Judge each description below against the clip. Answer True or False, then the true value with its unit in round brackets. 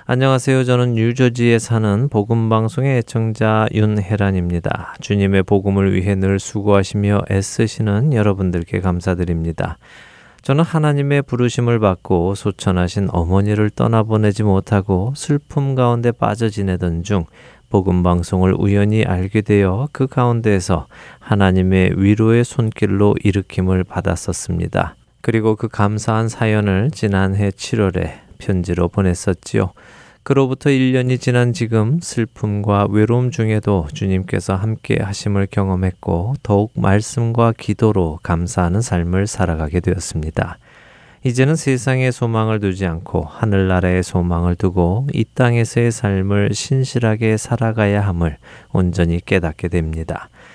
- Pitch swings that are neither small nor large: True (3.8 semitones)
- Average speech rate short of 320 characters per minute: True (305 characters per minute)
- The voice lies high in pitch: False (105 Hz)